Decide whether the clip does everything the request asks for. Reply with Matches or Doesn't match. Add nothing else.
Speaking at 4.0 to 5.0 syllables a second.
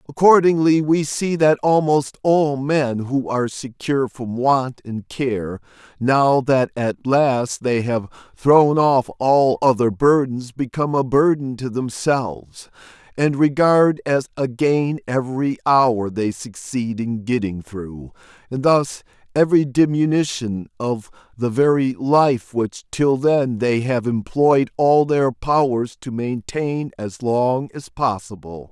Doesn't match